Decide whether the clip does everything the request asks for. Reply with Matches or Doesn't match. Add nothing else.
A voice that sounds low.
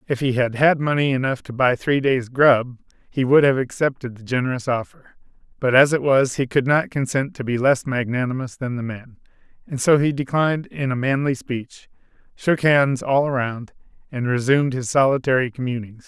Matches